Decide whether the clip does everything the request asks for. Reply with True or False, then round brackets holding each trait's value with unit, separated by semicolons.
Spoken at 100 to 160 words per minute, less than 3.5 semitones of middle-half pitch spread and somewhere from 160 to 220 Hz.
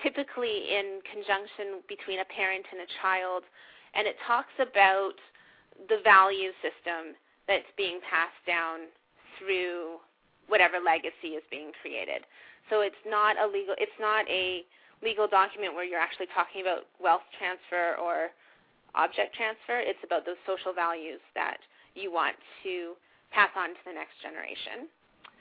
True (145 wpm; 2.9 semitones; 190 Hz)